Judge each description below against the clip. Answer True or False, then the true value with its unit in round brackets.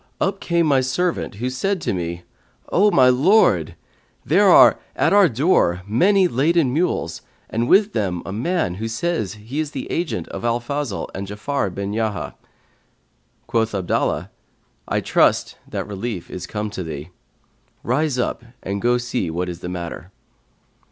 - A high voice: False (120 Hz)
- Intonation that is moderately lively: False (7.9 semitones)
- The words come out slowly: False (160 wpm)